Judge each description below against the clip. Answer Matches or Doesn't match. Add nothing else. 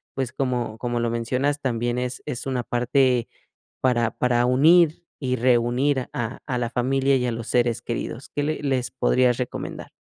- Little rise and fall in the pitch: Matches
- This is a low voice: Matches